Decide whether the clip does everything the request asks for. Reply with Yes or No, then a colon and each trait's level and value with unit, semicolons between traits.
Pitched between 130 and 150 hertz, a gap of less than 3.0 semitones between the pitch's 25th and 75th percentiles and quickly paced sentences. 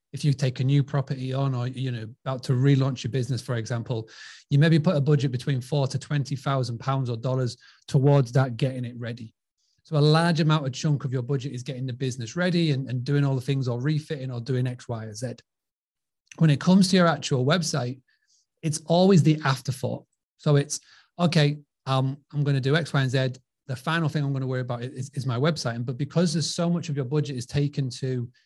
Yes: low, 135 Hz; narrow, 2.6 semitones; fast, 230 wpm